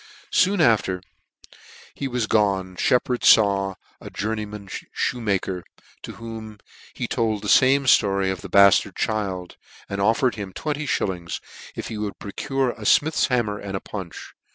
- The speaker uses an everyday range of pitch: Yes, average, 3.7 semitones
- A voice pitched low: Yes, low, 105 Hz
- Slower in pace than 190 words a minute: Yes, average, 155 wpm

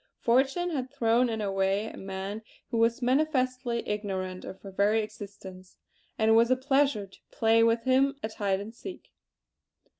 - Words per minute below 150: No, average, 175 wpm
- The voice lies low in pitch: No, high, 225 Hz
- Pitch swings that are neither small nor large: Yes, average, 4.2 semitones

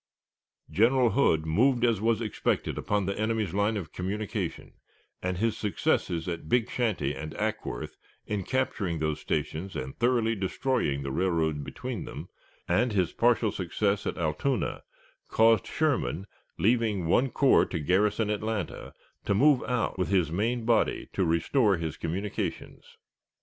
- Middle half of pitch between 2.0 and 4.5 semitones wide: No, average, 5.0 semitones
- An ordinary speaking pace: Yes, average, 145 wpm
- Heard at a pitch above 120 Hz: No, low, 105 Hz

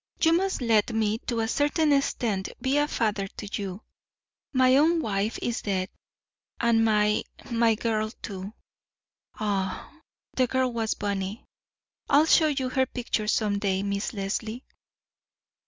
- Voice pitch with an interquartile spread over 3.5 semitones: Yes, average, 4.1 semitones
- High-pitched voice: Yes, high, 225 Hz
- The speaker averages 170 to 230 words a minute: No, average, 140 wpm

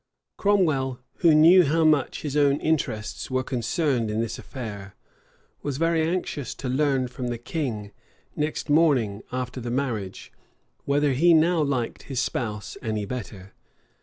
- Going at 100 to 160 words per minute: Yes, average, 145 wpm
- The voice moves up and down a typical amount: Yes, average, 4.7 semitones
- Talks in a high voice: No, low, 135 Hz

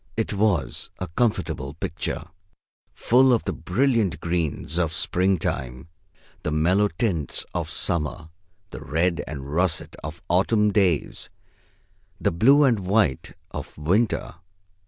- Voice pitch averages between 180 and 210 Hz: No, very low, 90 Hz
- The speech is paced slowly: Yes, slow, 120 wpm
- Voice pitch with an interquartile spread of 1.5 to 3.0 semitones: No, average, 5.1 semitones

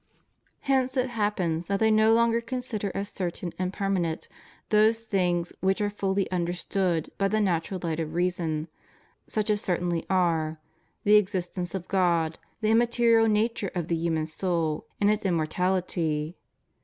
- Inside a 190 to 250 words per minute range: No, average, 155 wpm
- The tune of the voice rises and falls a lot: No, average, 3.8 semitones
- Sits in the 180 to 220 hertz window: Yes, high, 190 Hz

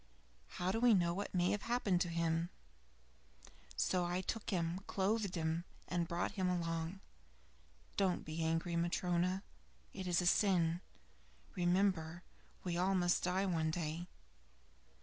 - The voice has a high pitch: No, medium, 175 Hz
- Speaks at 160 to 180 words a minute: No, average, 145 wpm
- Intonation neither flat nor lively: No, narrow, 2.1 semitones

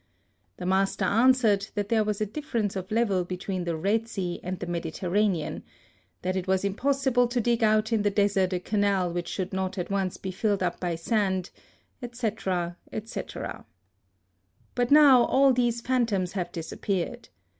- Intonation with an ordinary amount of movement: Yes, average, 3.7 semitones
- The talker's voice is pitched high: Yes, high, 200 Hz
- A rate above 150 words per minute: Yes, average, 175 wpm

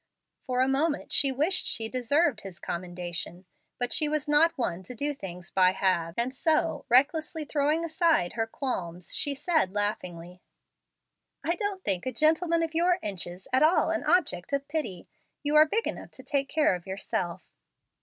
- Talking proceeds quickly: No, average, 175 wpm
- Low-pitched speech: No, very high, 265 Hz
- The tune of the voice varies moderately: No, wide, 8.7 semitones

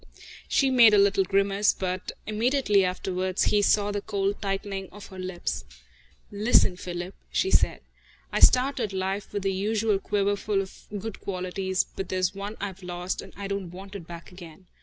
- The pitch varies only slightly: Yes, narrow, 1.8 semitones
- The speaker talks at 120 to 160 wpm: No, average, 170 wpm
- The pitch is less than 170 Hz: No, high, 195 Hz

